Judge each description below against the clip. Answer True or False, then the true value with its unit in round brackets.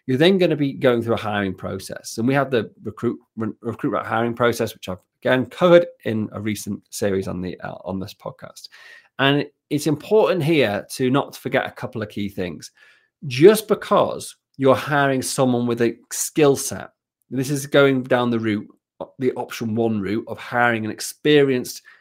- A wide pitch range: False (4.6 semitones)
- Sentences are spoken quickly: False (185 wpm)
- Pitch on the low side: True (120 Hz)